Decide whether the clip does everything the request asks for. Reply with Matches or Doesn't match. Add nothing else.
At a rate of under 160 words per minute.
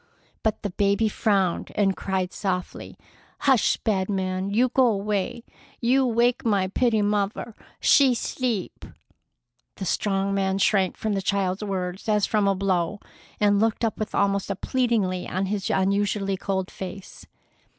Matches